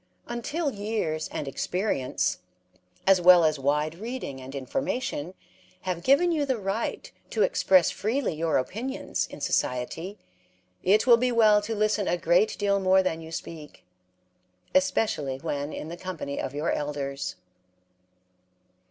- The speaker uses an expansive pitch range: Yes, wide, 6.8 semitones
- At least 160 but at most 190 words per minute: No, average, 140 wpm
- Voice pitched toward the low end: No, medium, 185 Hz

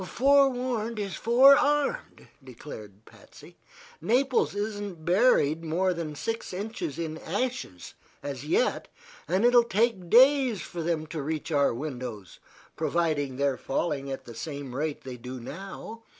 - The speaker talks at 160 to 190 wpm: No, average, 140 wpm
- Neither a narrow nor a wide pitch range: No, wide, 8.3 semitones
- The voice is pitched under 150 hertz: No, medium, 170 Hz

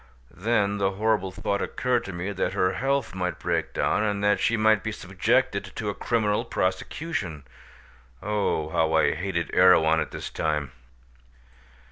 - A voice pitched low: Yes, low, 100 Hz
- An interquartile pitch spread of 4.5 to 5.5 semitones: No, average, 3.3 semitones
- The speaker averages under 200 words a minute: Yes, average, 155 wpm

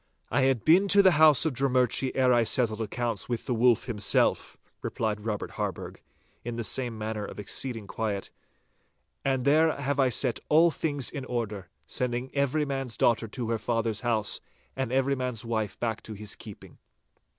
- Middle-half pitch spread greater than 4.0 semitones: No, average, 3.4 semitones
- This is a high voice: No, low, 120 Hz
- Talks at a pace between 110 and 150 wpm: No, average, 175 wpm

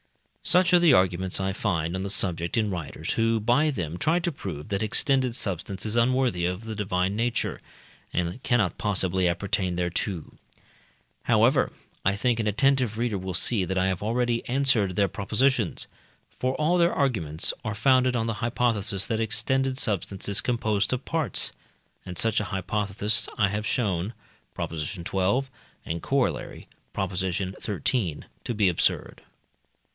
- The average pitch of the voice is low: Yes, low, 105 Hz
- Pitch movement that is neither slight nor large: Yes, average, 4.7 semitones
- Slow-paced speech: No, average, 155 wpm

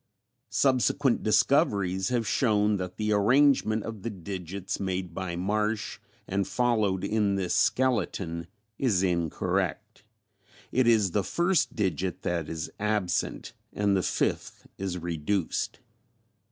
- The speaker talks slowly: Yes, slow, 120 wpm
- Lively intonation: No, average, 3.3 semitones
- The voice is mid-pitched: No, low, 100 Hz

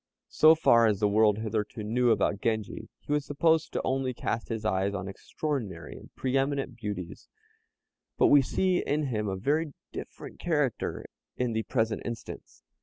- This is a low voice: Yes, low, 115 Hz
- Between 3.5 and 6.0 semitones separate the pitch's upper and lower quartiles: Yes, average, 4.9 semitones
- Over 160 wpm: Yes, average, 170 wpm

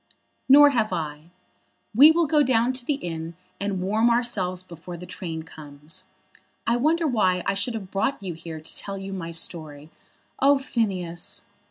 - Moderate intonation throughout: No, wide, 6.4 semitones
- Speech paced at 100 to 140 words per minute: No, average, 170 wpm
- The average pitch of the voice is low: No, high, 195 Hz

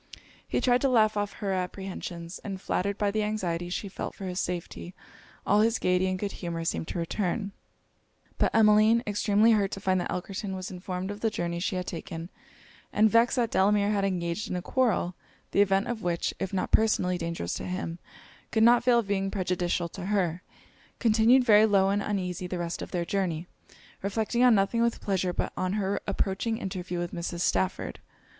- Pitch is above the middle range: Yes, high, 195 Hz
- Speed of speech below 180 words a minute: No, average, 195 wpm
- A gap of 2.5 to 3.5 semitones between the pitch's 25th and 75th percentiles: Yes, average, 2.9 semitones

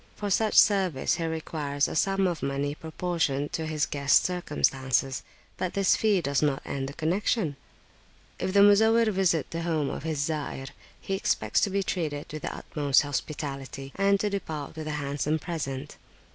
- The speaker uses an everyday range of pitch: Yes, average, 5.0 semitones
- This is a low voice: No, medium, 155 Hz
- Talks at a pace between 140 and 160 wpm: No, average, 175 wpm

